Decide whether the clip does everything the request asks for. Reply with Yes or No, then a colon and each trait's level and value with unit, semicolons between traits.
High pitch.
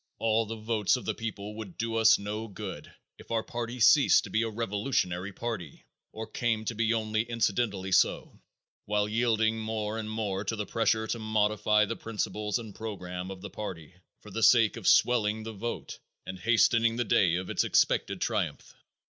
No: low, 110 Hz